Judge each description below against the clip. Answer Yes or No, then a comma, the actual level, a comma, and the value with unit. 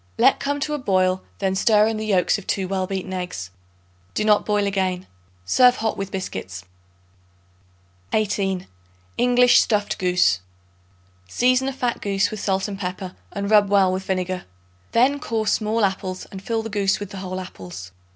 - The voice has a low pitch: No, high, 195 Hz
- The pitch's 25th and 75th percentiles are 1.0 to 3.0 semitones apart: Yes, average, 2.7 semitones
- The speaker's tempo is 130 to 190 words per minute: Yes, average, 170 wpm